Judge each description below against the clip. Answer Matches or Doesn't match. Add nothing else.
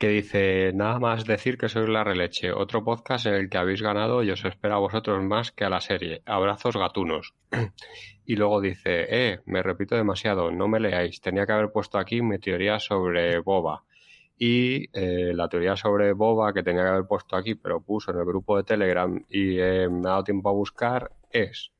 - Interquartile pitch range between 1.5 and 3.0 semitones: Matches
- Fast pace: Matches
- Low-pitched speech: Matches